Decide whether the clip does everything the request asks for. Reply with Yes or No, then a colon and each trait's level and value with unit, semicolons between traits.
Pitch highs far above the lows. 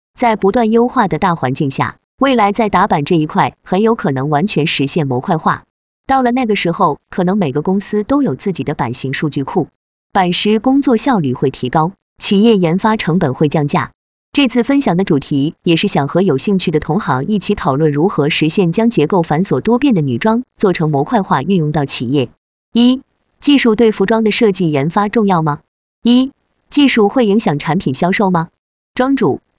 Yes: wide, 6.6 semitones